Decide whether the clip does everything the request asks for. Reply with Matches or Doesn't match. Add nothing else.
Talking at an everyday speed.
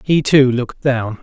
Matches